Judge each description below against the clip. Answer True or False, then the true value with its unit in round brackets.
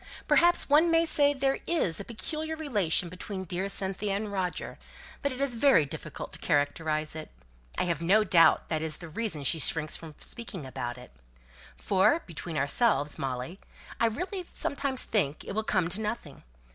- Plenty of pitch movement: True (8.2 semitones)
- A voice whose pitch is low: False (190 Hz)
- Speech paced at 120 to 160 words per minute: False (175 wpm)